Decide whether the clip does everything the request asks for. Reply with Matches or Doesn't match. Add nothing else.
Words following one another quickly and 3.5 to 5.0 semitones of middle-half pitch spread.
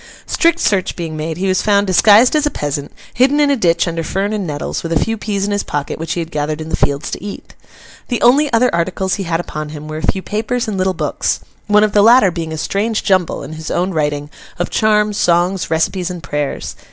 Matches